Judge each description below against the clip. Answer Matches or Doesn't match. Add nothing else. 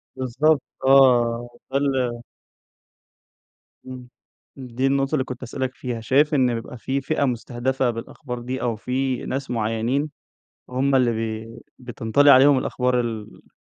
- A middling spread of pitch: Doesn't match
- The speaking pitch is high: Doesn't match